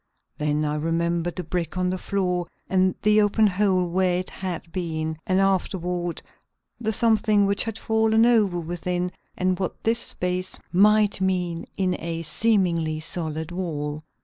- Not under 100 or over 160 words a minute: Yes, average, 150 wpm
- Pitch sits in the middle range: Yes, medium, 180 Hz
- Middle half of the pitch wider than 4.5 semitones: No, average, 2.9 semitones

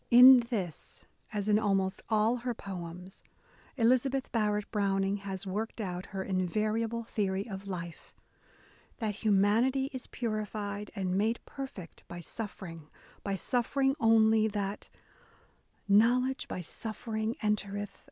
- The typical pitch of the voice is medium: No, high, 210 Hz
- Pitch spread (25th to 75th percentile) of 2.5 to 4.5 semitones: Yes, average, 2.9 semitones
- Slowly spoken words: Yes, slow, 125 wpm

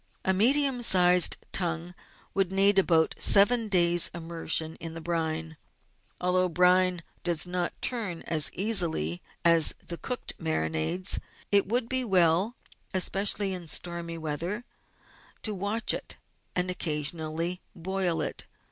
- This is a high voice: No, medium, 180 Hz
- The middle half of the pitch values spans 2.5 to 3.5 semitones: Yes, average, 3.0 semitones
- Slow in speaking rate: Yes, slow, 130 wpm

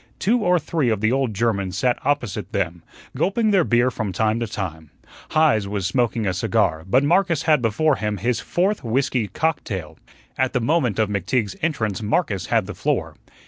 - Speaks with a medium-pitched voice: No, low, 120 Hz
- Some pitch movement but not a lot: No, wide, 6.8 semitones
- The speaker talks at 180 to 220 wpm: Yes, average, 185 wpm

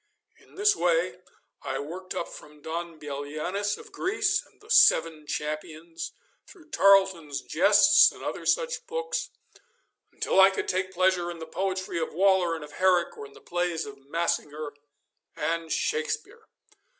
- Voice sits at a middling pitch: Yes, medium, 180 Hz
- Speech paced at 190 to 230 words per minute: No, average, 150 wpm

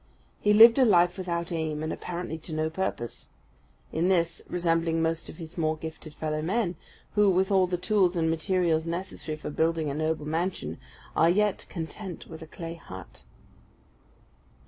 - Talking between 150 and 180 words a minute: Yes, average, 170 wpm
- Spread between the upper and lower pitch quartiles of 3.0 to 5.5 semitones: No, narrow, 2.4 semitones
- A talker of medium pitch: Yes, medium, 165 Hz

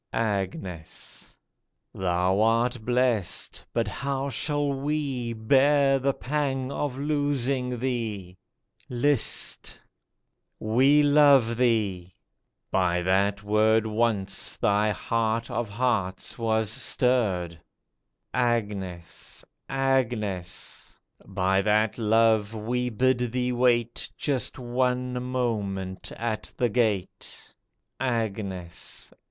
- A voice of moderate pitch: No, low, 115 Hz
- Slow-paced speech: Yes, slow, 95 wpm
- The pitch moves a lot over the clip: No, average, 3.9 semitones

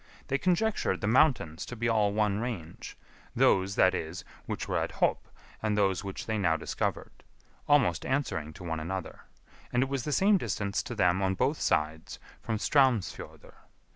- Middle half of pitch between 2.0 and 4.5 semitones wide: No, wide, 5.5 semitones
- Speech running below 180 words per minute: Yes, average, 170 wpm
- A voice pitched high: No, low, 105 Hz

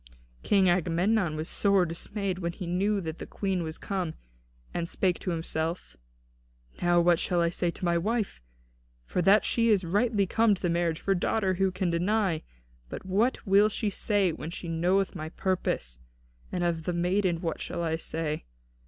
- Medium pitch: Yes, medium, 180 Hz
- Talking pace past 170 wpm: Yes, average, 190 wpm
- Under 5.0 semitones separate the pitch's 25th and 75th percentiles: Yes, average, 2.8 semitones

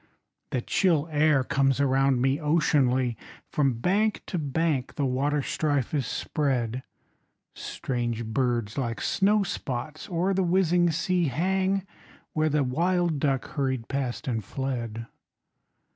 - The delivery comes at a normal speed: No, slow, 120 wpm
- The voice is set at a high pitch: No, medium, 140 Hz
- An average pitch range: Yes, average, 4.7 semitones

